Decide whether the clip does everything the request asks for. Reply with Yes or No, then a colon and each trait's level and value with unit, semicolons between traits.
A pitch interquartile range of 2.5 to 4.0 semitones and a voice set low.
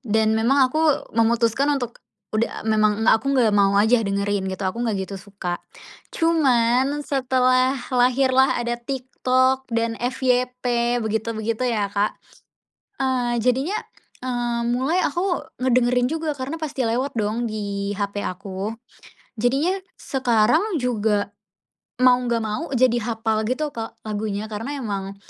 No: average, 3.2 semitones; high, 240 Hz